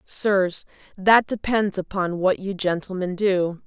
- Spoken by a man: No, female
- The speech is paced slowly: Yes, slow, 130 wpm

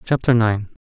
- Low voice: Yes, low, 115 Hz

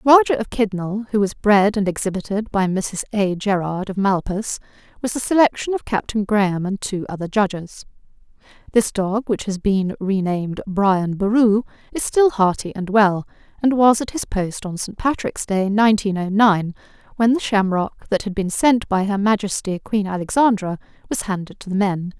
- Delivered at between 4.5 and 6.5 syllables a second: Yes, 4.9 syllables/s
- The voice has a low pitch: No, high, 205 Hz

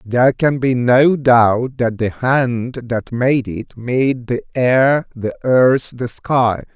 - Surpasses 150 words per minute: Yes, average, 160 wpm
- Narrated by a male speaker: Yes, male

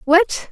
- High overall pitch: Yes, very high, 330 Hz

